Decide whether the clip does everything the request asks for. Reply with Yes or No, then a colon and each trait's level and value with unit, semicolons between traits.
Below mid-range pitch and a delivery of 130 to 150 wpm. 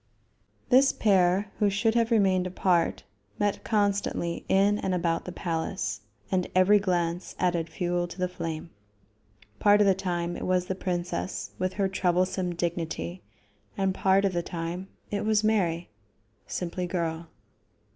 No: medium, 185 Hz; average, 145 wpm